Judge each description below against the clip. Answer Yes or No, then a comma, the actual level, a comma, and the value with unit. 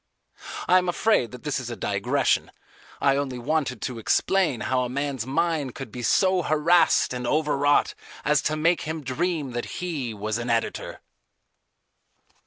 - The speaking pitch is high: No, medium, 140 Hz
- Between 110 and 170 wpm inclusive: Yes, average, 160 wpm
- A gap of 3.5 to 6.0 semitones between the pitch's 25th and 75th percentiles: Yes, average, 4.4 semitones